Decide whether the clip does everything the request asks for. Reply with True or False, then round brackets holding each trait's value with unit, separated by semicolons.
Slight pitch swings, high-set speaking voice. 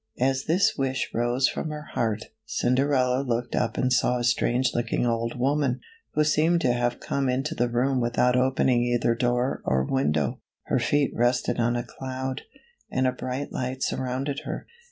False (1.8 semitones; 125 Hz)